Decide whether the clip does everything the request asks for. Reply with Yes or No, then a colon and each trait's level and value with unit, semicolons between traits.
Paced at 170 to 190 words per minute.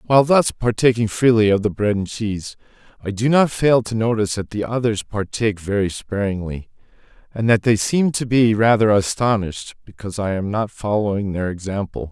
Yes: average, 180 wpm